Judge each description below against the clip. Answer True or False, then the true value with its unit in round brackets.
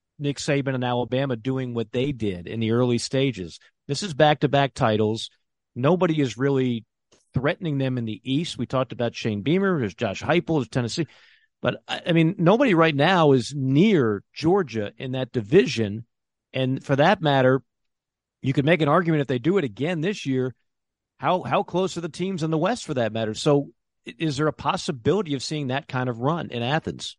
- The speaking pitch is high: False (140 Hz)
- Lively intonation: False (4.9 semitones)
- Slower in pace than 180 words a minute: False (195 wpm)